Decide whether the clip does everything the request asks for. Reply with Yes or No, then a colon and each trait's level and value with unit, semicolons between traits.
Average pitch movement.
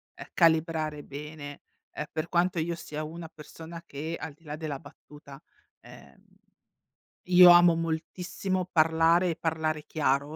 No: narrow, 1.9 semitones